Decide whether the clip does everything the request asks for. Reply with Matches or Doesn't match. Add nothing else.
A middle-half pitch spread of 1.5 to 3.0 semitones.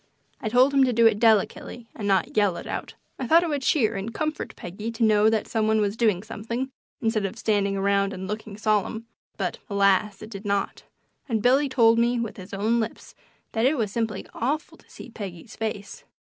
Matches